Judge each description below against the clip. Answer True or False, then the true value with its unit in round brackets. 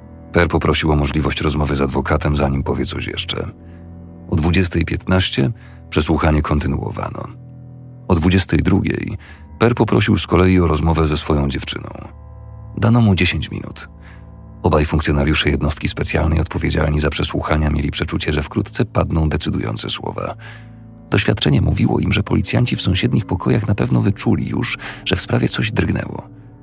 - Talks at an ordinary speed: True (135 wpm)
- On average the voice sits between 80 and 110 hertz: True (85 Hz)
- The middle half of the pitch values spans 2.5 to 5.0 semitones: False (5.5 semitones)